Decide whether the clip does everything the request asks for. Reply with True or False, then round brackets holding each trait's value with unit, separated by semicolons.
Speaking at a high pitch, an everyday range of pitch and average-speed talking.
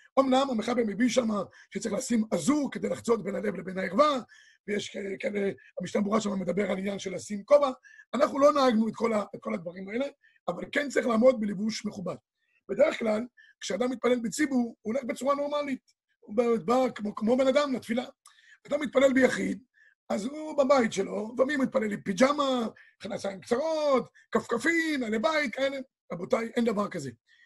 False (245 Hz; 4.8 semitones; 175 wpm)